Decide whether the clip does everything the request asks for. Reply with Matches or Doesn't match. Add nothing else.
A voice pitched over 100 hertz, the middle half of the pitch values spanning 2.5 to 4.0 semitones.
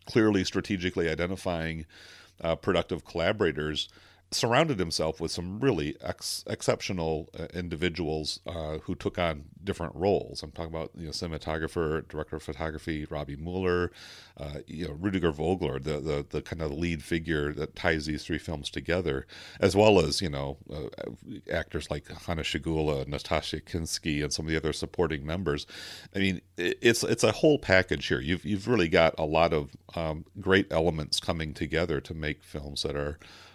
Doesn't match